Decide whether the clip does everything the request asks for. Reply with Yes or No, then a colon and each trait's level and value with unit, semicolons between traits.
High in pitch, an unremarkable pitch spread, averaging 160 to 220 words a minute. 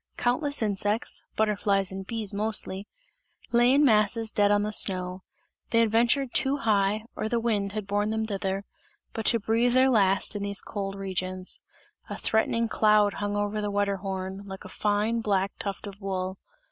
No: high, 205 Hz; narrow, 2.2 semitones; average, 170 wpm